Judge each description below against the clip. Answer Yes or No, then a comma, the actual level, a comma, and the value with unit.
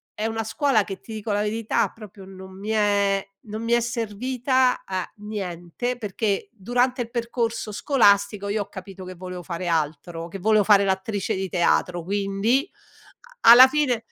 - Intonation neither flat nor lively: Yes, average, 3.4 semitones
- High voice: Yes, high, 205 Hz